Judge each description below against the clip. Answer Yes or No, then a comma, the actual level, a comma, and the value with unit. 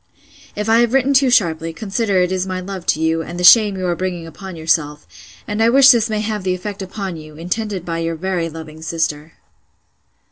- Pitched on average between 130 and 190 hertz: Yes, medium, 185 Hz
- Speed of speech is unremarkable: No, fast, 215 wpm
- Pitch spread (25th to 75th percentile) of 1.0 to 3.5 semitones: No, average, 4.3 semitones